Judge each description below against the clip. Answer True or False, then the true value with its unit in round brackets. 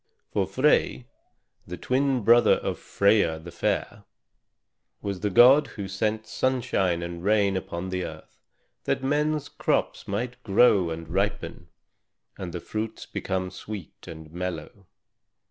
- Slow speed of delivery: True (130 wpm)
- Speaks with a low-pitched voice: True (100 Hz)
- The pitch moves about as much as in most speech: True (4.4 semitones)